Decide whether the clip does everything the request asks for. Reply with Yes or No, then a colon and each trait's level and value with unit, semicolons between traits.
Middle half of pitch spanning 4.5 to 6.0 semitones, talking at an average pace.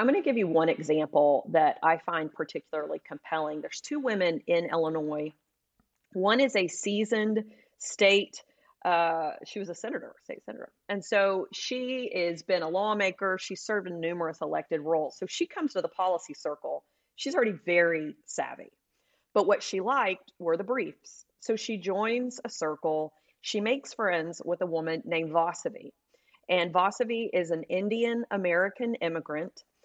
Yes: wide, 5.4 semitones; average, 160 wpm